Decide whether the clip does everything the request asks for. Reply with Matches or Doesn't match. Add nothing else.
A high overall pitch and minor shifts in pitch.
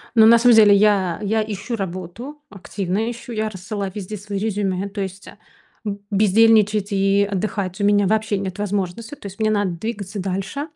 Matches